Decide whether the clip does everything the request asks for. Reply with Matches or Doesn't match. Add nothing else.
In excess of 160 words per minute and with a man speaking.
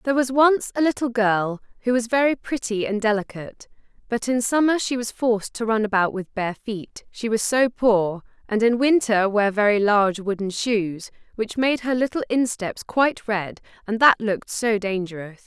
Doesn't match